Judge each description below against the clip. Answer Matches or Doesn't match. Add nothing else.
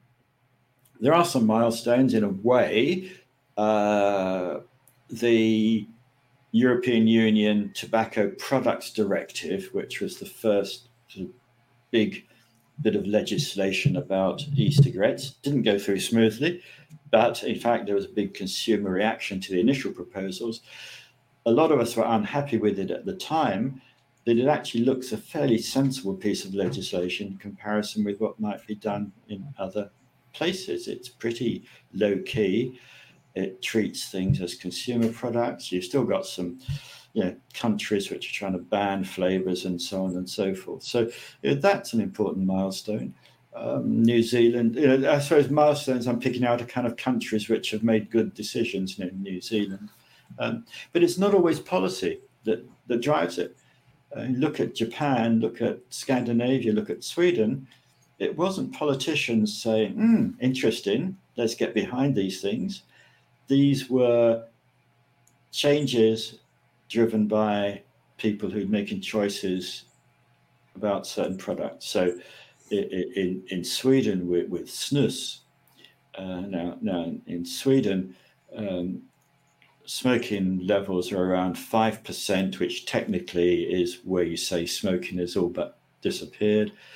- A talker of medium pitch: Doesn't match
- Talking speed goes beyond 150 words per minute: Doesn't match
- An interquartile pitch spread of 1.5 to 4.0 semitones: Doesn't match